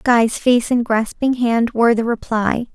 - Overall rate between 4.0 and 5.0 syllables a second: Yes, 4.3 syllables/s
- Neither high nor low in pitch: No, high, 230 Hz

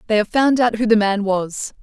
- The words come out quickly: Yes, fast, 265 wpm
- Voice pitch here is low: No, high, 215 Hz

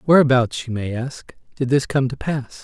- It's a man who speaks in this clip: Yes, male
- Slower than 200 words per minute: No, fast, 205 wpm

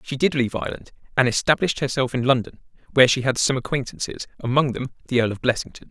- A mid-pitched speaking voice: No, low, 130 Hz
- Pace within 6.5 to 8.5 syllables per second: Yes, 6.9 syllables/s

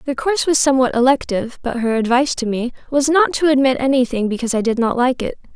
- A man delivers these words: No, female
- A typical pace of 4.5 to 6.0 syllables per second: No, 6.7 syllables/s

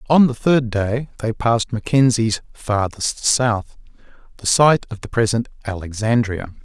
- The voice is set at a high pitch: No, low, 115 Hz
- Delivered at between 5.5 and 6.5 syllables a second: No, 4.3 syllables/s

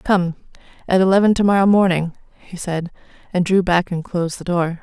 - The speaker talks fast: No, average, 160 wpm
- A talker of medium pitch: Yes, medium, 180 Hz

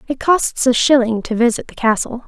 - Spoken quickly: Yes, fast, 210 wpm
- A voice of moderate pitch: No, high, 245 Hz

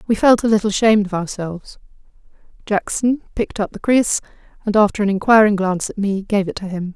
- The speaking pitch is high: Yes, high, 205 Hz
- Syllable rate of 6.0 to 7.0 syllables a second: Yes, 6.3 syllables/s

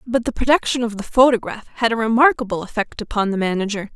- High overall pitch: Yes, high, 225 Hz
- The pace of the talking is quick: No, average, 195 wpm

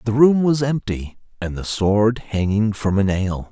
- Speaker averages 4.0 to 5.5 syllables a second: Yes, 4.1 syllables/s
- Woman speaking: No, male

